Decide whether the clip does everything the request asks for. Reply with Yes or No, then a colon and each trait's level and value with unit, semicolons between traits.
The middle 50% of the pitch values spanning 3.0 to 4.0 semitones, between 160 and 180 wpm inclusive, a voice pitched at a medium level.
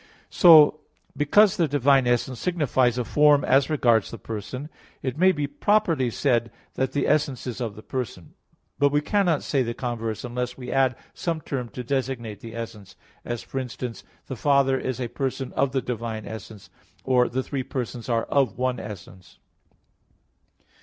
No: average, 3.3 semitones; average, 170 wpm; low, 130 Hz